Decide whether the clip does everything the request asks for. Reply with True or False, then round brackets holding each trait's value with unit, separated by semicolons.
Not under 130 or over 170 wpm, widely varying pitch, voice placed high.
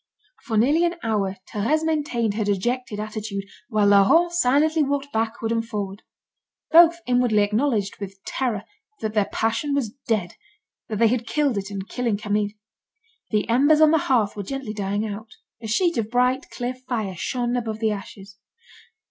False (165 wpm; 4.2 semitones; 225 Hz)